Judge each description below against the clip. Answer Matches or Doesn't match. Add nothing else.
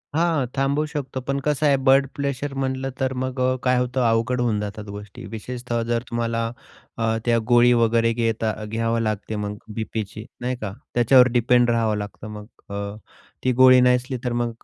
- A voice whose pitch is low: Matches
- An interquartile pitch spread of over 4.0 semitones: Doesn't match